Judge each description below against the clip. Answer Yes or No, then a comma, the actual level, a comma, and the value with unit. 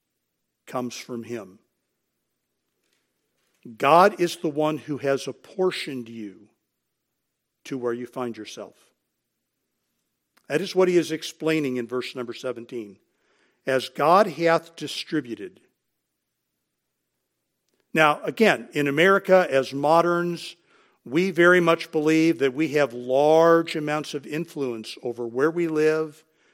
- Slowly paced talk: Yes, slow, 115 wpm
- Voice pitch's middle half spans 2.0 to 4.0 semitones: No, average, 4.8 semitones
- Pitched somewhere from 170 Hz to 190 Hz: No, medium, 150 Hz